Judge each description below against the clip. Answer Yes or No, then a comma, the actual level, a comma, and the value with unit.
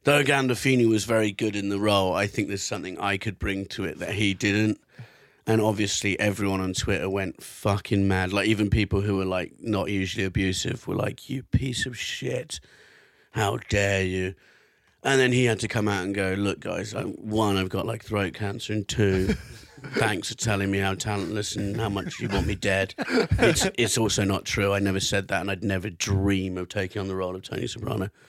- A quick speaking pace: Yes, fast, 210 wpm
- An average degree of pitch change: No, narrow, 1.9 semitones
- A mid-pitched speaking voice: No, low, 100 Hz